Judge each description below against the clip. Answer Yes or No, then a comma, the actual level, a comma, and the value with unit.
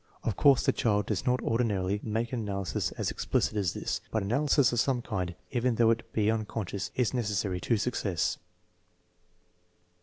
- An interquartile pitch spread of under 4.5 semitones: Yes, average, 3.2 semitones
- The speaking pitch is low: Yes, low, 110 Hz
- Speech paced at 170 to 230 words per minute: Yes, average, 175 wpm